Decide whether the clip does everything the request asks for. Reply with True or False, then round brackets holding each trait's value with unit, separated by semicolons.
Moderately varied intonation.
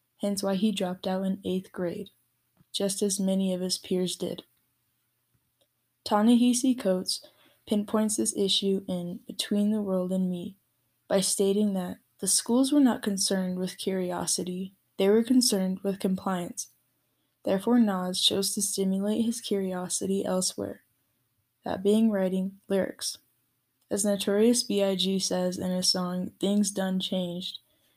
False (2.1 semitones)